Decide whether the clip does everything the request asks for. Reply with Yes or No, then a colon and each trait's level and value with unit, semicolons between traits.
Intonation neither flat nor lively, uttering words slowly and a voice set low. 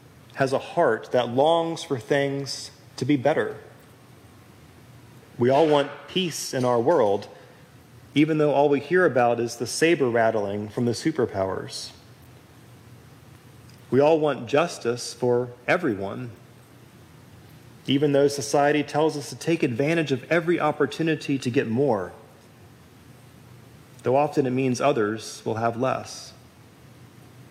Yes: average, 3.2 semitones; slow, 125 wpm; low, 130 Hz